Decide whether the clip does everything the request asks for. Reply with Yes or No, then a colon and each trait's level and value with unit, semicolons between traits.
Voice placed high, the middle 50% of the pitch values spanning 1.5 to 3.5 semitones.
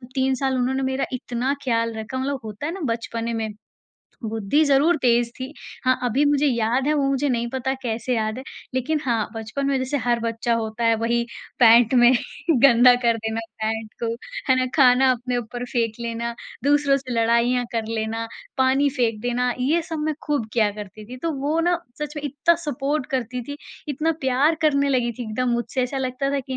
Yes: very high, 250 Hz; average, 3.0 semitones